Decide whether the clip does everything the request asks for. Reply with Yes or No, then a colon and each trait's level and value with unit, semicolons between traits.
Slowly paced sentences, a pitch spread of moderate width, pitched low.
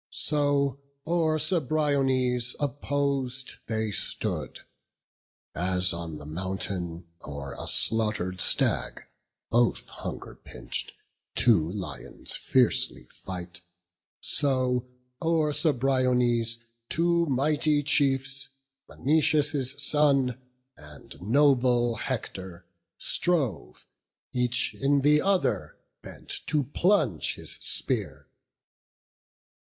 No: slow, 85 wpm; wide, 6.7 semitones; low, 130 Hz